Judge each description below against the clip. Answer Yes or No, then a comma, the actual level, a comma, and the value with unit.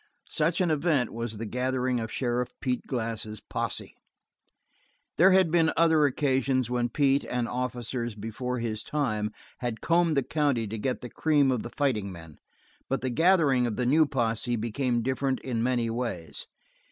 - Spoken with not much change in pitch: No, average, 3.5 semitones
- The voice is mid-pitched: No, low, 125 Hz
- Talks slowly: No, average, 165 wpm